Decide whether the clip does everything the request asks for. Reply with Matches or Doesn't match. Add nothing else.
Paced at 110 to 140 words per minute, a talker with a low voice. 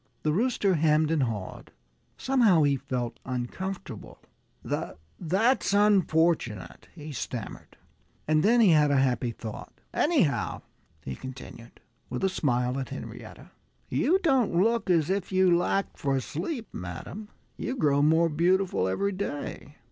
Doesn't match